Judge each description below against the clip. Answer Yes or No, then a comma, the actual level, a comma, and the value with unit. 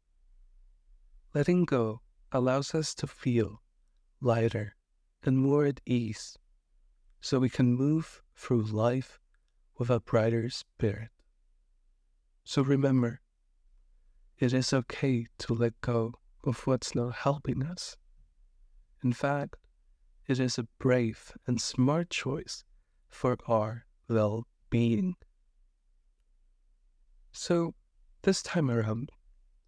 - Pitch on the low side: Yes, low, 115 Hz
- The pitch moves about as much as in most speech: No, wide, 7.7 semitones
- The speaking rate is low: Yes, slow, 105 wpm